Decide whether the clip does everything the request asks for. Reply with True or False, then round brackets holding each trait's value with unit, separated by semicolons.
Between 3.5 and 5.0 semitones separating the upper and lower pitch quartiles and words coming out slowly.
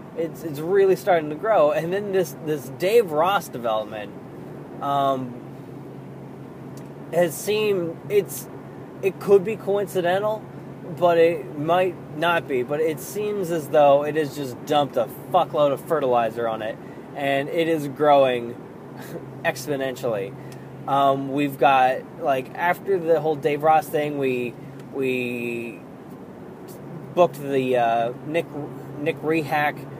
True (4.2 semitones; 130 wpm)